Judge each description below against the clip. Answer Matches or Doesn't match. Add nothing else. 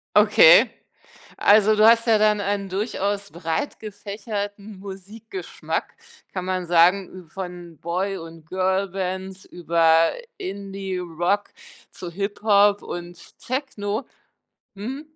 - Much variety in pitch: Doesn't match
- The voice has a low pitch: Doesn't match